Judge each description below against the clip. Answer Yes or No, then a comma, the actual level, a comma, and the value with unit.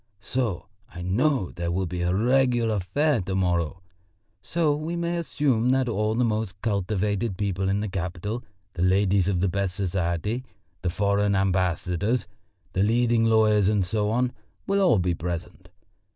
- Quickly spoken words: No, average, 160 wpm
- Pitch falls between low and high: No, low, 100 Hz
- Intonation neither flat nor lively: Yes, average, 4.4 semitones